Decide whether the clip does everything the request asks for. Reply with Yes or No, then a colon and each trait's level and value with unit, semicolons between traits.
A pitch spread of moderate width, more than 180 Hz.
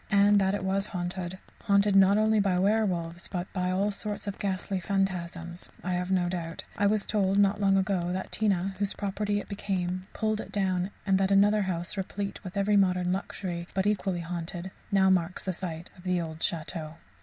No: narrow, 2.0 semitones; high, 190 Hz